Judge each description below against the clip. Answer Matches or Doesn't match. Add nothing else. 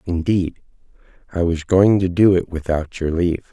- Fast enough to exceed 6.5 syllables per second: Doesn't match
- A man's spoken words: Matches